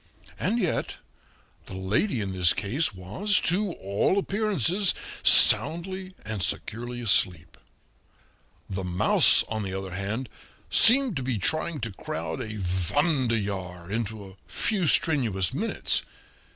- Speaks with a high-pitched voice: No, low, 115 Hz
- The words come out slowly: Yes, slow, 125 wpm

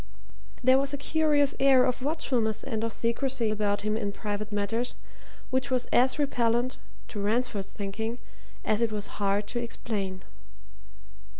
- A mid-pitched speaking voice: No, high, 230 Hz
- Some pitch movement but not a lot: Yes, average, 3.7 semitones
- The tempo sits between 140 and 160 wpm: Yes, average, 145 wpm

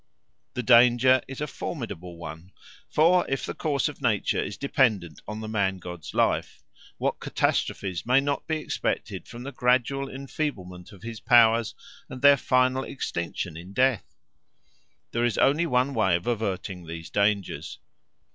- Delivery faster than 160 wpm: No, average, 155 wpm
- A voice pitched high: No, low, 115 Hz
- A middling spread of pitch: No, wide, 5.8 semitones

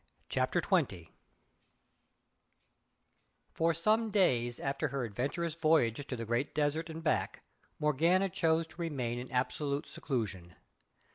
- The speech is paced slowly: Yes, slow, 120 wpm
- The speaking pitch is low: No, medium, 145 Hz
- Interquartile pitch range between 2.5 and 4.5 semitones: No, average, 5.2 semitones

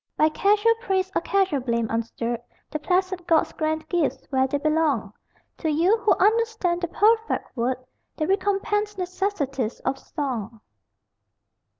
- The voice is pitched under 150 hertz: No, very high, 325 Hz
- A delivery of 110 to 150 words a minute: Yes, slow, 135 wpm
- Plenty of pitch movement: Yes, wide, 6.7 semitones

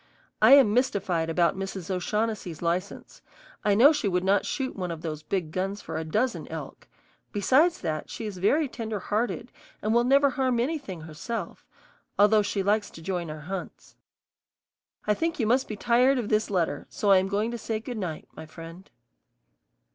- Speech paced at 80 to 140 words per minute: No, average, 185 wpm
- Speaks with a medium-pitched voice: No, high, 205 Hz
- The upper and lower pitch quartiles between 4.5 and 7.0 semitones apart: Yes, average, 4.8 semitones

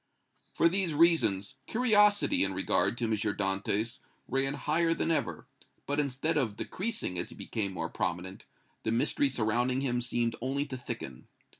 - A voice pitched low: Yes, low, 125 Hz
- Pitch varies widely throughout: Yes, wide, 6.7 semitones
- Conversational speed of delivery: Yes, average, 155 wpm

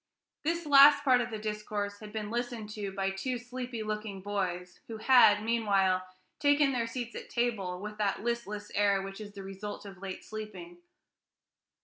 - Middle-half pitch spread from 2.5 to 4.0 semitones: Yes, average, 3.3 semitones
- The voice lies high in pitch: Yes, high, 215 Hz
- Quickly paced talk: No, average, 170 wpm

